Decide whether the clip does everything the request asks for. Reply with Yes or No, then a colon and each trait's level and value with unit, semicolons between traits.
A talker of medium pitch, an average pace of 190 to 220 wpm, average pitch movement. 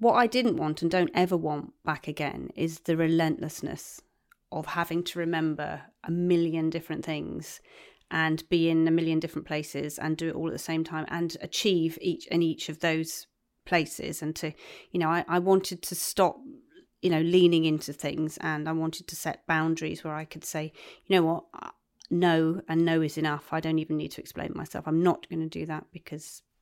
No: medium, 165 Hz; fast, 205 wpm; narrow, 1.7 semitones